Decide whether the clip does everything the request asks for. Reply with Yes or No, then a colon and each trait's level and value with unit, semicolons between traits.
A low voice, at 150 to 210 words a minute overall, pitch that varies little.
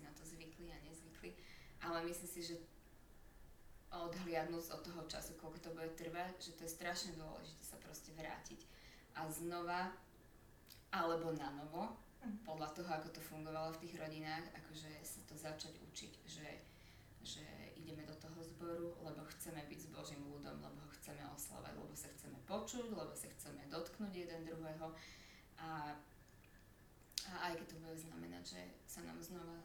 No: medium, 160 Hz; average, 160 wpm; narrow, 2.2 semitones